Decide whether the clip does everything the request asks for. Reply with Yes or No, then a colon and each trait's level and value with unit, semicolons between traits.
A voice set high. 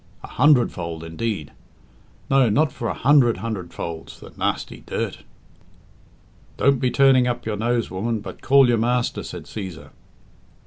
No: low, 115 Hz